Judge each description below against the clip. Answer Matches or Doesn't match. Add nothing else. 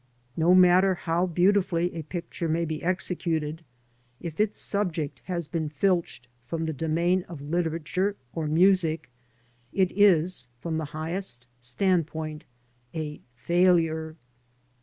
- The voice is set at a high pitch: Doesn't match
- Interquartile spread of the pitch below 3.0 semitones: Matches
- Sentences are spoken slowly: Matches